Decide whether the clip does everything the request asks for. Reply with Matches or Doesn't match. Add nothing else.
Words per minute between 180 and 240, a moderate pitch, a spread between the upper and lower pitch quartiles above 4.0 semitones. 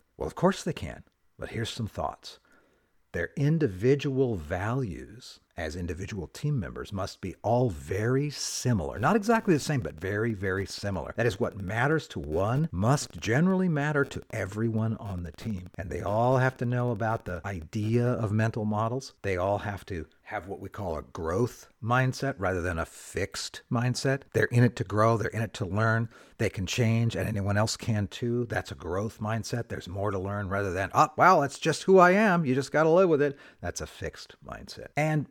Doesn't match